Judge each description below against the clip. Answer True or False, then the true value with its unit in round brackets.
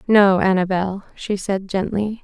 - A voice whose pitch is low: False (195 Hz)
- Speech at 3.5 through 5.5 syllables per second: True (4.1 syllables/s)